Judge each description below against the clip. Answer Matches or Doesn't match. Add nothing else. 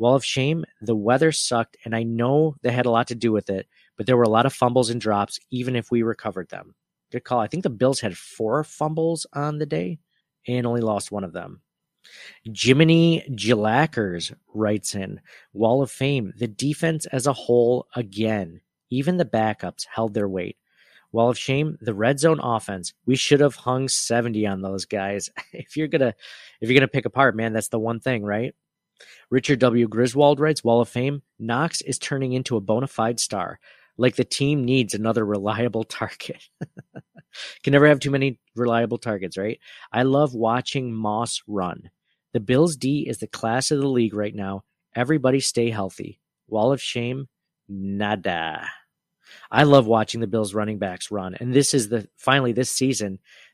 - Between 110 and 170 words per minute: Doesn't match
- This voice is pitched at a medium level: Doesn't match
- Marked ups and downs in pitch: Doesn't match